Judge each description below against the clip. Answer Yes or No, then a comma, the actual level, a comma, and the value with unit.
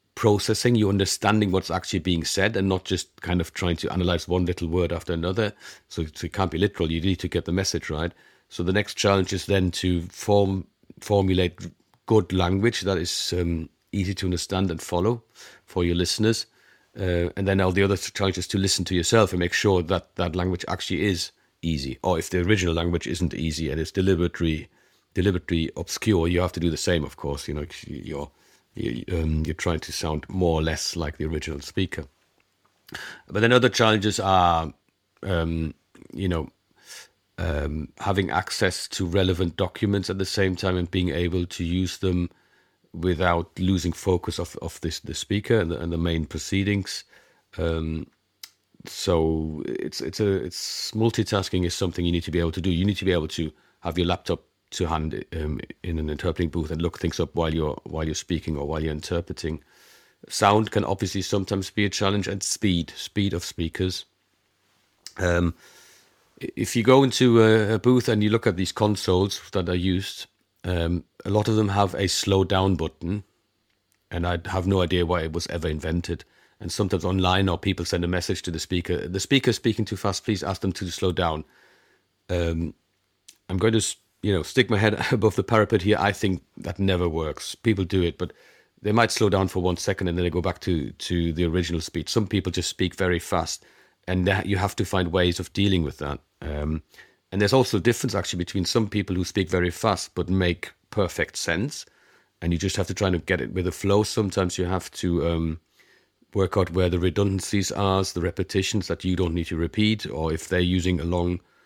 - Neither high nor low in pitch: No, very low, 90 Hz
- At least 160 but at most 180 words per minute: No, fast, 205 wpm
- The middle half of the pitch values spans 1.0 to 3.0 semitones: Yes, average, 2.7 semitones